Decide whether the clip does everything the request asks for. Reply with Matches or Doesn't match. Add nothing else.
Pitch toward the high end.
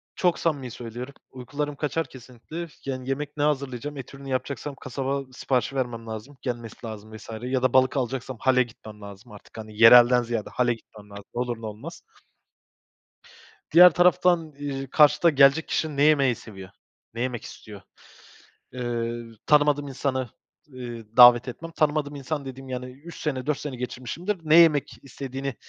Doesn't match